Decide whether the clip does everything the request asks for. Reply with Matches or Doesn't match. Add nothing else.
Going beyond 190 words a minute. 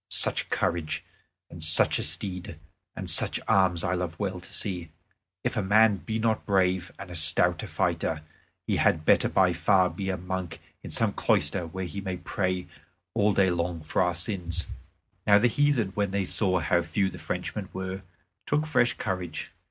Doesn't match